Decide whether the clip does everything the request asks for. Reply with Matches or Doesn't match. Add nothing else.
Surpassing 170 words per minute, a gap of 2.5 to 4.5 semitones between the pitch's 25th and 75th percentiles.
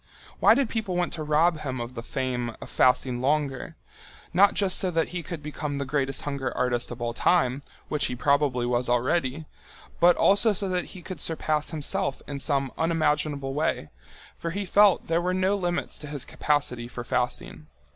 Doesn't match